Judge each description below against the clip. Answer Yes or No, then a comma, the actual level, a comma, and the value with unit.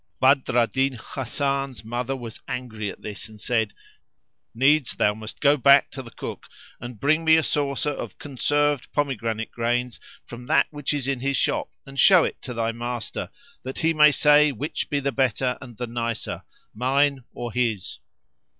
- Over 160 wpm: Yes, average, 180 wpm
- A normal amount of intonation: Yes, average, 3.3 semitones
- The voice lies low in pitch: Yes, low, 130 Hz